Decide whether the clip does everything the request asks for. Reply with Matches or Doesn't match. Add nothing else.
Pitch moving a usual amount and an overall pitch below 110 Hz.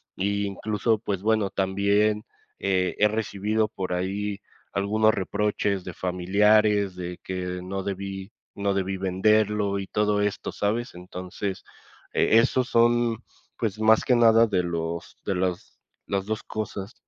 Doesn't match